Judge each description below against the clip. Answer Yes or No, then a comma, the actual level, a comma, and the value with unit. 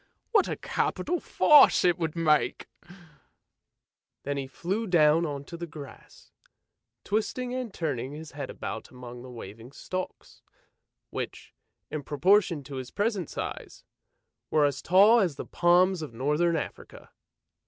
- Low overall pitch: No, medium, 160 Hz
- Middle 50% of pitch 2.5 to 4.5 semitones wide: No, average, 5.1 semitones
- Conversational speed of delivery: Yes, average, 145 wpm